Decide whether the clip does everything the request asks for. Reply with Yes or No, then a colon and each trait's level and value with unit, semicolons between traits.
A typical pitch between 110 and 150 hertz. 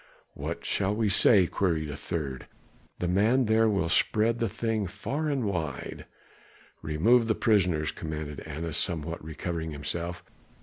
No: very low, 90 Hz